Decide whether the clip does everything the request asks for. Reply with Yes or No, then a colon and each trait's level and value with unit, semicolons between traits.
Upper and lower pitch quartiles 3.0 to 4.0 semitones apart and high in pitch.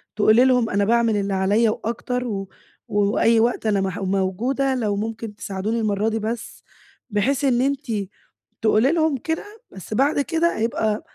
Yes: average, 3.4 semitones; high, 225 Hz